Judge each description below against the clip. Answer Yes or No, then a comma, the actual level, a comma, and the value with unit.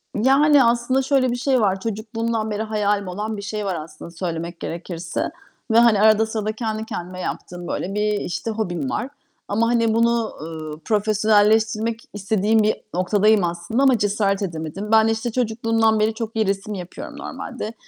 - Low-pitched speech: No, high, 215 Hz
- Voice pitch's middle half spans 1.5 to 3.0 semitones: Yes, average, 2.7 semitones